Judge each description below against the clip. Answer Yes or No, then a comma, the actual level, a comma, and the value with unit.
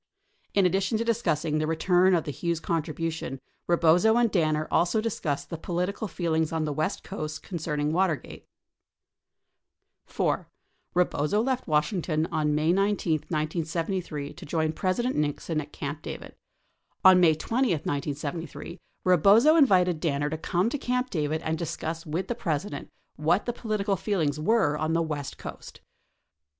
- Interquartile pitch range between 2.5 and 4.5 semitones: Yes, average, 3.9 semitones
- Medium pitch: Yes, medium, 165 Hz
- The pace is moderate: Yes, average, 150 wpm